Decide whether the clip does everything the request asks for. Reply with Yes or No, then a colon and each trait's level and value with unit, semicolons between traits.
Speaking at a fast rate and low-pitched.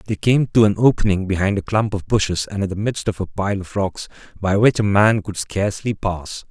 Yes: fast, 240 wpm; low, 100 Hz